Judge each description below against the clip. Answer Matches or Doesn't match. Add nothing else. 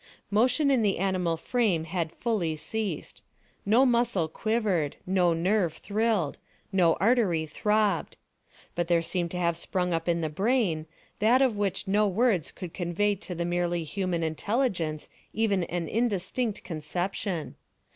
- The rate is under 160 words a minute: Matches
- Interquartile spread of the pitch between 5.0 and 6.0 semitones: Doesn't match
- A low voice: Doesn't match